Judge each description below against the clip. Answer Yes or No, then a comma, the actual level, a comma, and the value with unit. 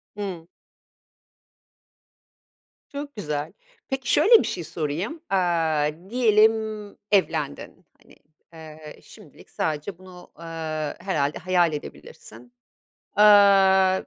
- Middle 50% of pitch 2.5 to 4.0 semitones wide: No, average, 4.6 semitones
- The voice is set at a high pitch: No, medium, 175 Hz